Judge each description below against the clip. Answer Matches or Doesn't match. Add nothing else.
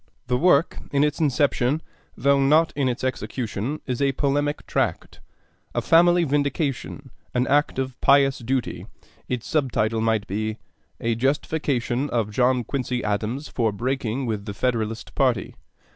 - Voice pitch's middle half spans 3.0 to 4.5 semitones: Matches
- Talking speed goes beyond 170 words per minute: Doesn't match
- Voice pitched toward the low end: Matches